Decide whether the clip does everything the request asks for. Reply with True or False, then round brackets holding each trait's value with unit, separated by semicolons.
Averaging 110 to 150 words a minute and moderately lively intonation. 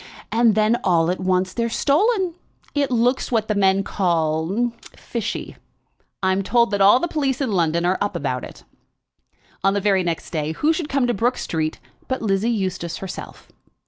False (175 wpm; 4.9 semitones)